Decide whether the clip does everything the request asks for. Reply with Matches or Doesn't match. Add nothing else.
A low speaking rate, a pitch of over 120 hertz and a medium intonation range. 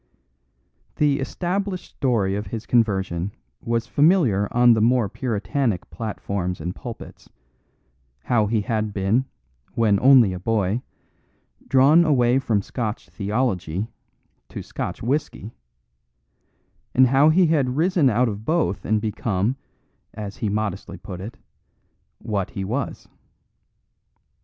Doesn't match